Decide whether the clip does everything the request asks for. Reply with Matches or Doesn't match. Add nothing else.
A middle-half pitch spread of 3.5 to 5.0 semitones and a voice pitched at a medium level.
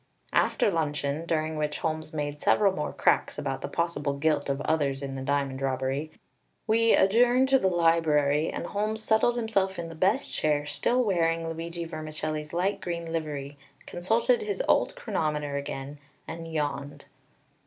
Matches